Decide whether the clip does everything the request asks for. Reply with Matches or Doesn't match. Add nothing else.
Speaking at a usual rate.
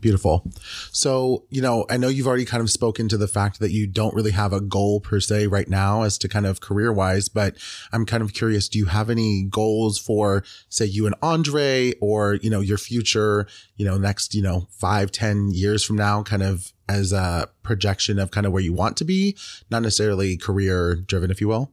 Doesn't match